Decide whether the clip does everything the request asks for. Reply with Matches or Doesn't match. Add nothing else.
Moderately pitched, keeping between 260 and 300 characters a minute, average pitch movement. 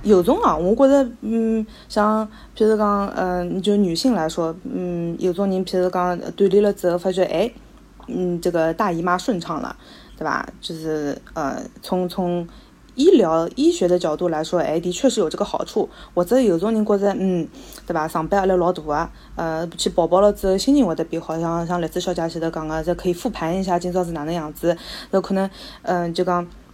Matches